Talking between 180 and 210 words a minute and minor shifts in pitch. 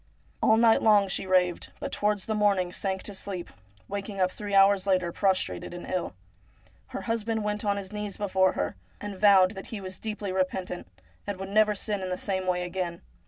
Yes: average, 200 wpm; narrow, 2.0 semitones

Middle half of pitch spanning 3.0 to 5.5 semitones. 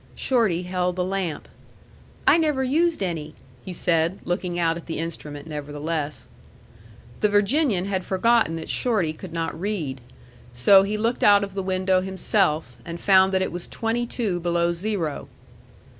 Yes: average, 3.7 semitones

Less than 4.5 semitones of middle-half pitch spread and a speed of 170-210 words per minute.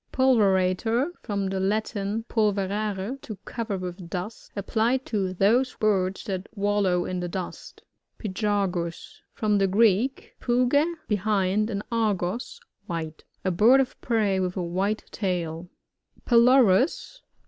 No: average, 3.6 semitones; slow, 135 wpm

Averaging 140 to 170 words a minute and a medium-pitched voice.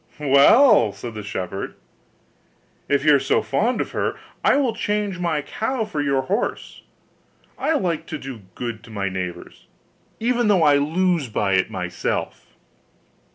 Yes: average, 155 wpm; medium, 145 Hz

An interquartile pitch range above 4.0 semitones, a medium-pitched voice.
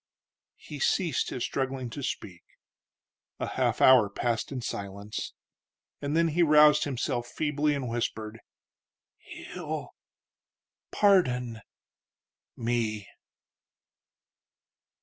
No: average, 4.5 semitones; low, 125 Hz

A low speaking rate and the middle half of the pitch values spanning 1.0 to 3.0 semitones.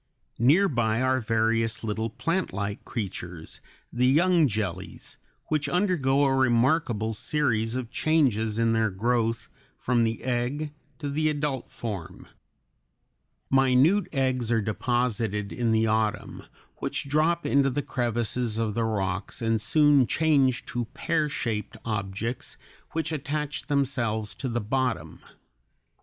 No: slow, 125 wpm; average, 4.1 semitones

